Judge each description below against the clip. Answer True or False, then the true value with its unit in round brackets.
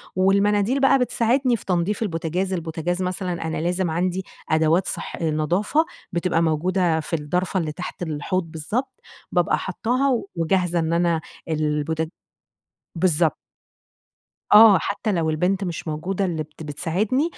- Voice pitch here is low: False (175 Hz)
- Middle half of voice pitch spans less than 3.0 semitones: False (3.4 semitones)